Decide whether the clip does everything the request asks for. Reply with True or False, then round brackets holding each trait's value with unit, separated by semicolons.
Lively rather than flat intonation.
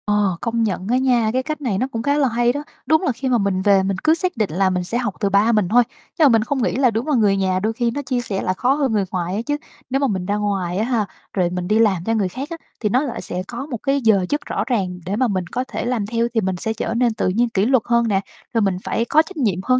False (4.5 semitones)